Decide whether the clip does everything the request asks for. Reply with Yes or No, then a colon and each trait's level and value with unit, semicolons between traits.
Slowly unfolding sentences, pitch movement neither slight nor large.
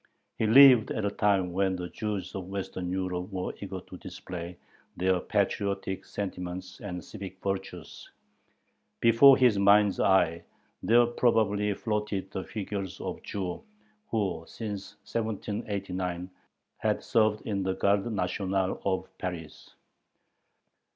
No: slow, 125 wpm; narrow, 2.3 semitones